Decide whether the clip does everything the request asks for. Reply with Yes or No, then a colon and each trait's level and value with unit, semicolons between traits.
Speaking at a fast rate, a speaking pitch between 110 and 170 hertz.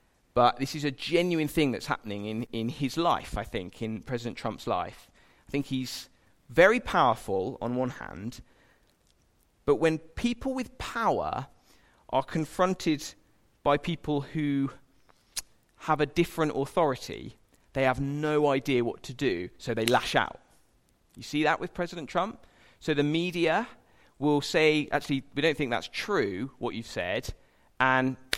No: average, 150 wpm; medium, 140 Hz